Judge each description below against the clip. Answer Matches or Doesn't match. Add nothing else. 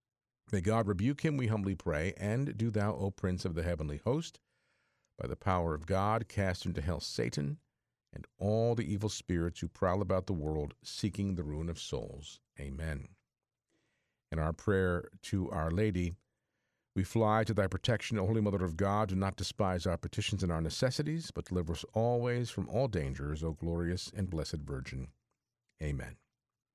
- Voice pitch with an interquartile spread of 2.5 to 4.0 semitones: Doesn't match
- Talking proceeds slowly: Doesn't match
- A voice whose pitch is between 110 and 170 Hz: Doesn't match